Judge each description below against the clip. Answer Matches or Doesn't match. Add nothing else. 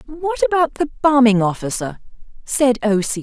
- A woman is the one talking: Matches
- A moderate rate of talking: Matches